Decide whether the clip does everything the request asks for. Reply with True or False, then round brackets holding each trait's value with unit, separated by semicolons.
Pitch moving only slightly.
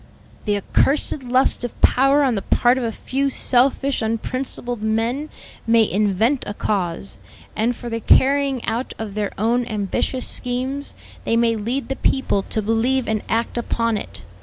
False (3.2 semitones)